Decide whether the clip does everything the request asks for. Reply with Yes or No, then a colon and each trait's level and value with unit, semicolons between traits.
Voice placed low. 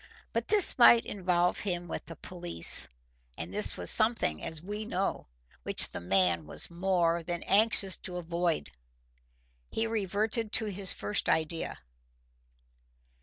No: medium, 175 Hz